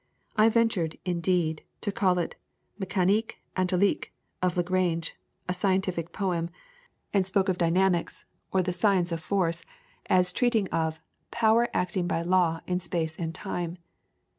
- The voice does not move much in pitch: Yes, narrow, 2.2 semitones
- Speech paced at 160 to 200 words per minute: No, average, 140 wpm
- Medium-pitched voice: Yes, medium, 180 Hz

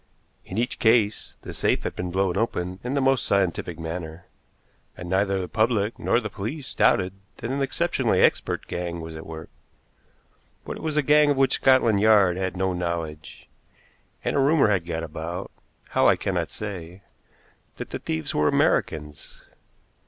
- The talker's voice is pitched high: No, very low, 95 Hz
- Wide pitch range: Yes, wide, 5.8 semitones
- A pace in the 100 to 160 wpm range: No, average, 170 wpm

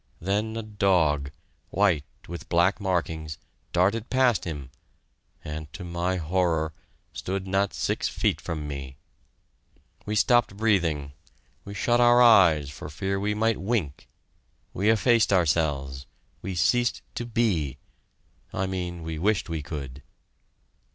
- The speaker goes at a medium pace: No, slow, 130 wpm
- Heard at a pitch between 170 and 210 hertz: No, very low, 90 Hz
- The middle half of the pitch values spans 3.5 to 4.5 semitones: No, average, 5.1 semitones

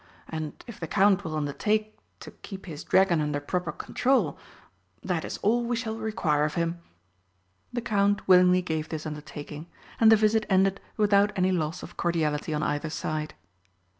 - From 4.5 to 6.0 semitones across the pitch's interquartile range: Yes, average, 5.1 semitones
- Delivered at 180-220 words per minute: No, average, 165 wpm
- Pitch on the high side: No, medium, 180 Hz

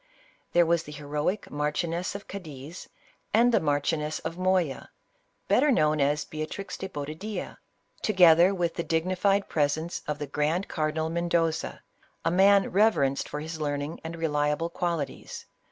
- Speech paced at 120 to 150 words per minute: Yes, average, 140 wpm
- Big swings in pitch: No, average, 3.4 semitones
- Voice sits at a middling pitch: Yes, medium, 165 Hz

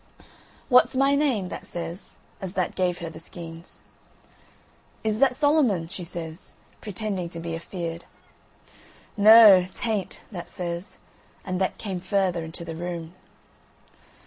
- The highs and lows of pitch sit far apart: No, average, 3.9 semitones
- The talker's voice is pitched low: No, medium, 180 Hz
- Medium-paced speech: No, slow, 130 wpm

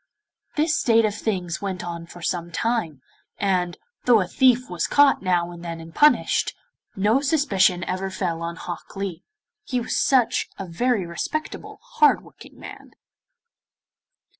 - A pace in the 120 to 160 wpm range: Yes, average, 150 wpm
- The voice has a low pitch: No, high, 190 Hz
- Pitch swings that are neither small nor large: No, wide, 5.8 semitones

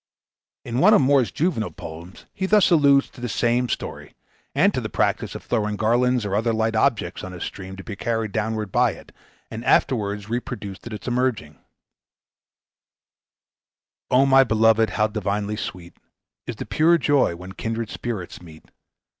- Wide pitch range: No, average, 3.8 semitones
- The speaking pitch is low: Yes, low, 110 Hz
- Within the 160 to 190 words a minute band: Yes, average, 165 wpm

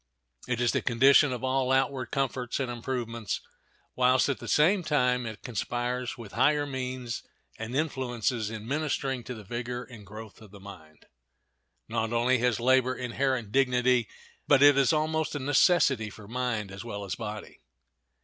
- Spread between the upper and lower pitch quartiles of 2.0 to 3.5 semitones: Yes, average, 2.8 semitones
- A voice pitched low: Yes, low, 125 Hz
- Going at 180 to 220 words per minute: No, average, 165 wpm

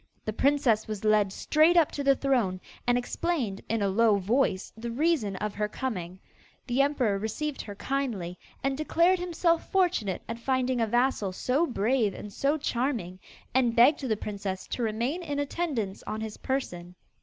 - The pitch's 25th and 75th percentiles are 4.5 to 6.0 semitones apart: Yes, average, 5.1 semitones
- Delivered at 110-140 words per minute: No, average, 170 wpm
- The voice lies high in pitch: Yes, high, 240 Hz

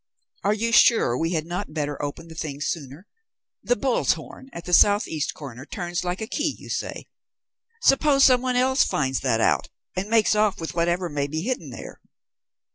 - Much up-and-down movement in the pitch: Yes, wide, 7.1 semitones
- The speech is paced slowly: No, average, 195 wpm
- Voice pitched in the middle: Yes, medium, 175 Hz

